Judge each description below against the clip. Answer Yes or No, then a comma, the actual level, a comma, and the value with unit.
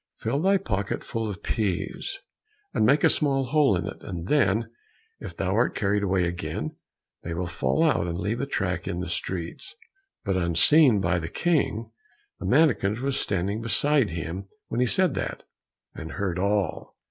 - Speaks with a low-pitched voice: Yes, low, 100 Hz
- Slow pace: No, average, 175 wpm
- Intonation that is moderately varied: No, wide, 7.4 semitones